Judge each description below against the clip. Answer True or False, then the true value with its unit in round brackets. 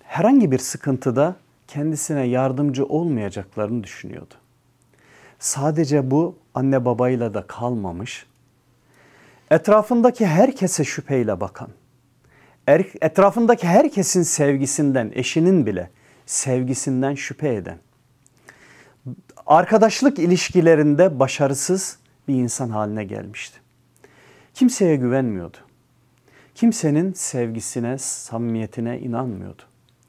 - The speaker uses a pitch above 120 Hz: True (135 Hz)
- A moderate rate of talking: False (75 wpm)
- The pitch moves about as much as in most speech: True (4.3 semitones)